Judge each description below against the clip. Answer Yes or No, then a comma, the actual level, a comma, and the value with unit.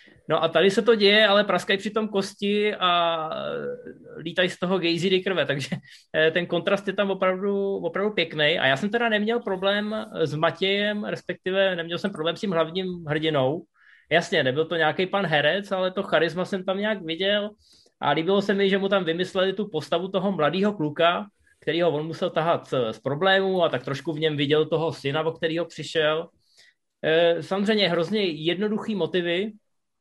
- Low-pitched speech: No, medium, 185 Hz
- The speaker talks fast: Yes, fast, 175 wpm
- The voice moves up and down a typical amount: Yes, average, 3.5 semitones